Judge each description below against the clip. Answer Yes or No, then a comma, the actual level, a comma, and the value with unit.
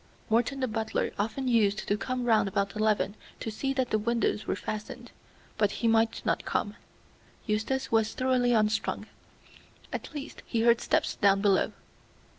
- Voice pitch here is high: Yes, high, 225 Hz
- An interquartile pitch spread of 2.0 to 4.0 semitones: Yes, narrow, 2.5 semitones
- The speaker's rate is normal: Yes, average, 160 wpm